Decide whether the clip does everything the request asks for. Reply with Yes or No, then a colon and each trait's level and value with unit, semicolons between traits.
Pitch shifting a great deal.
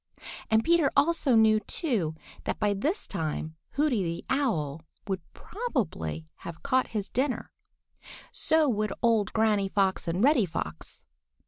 Yes: wide, 7.7 semitones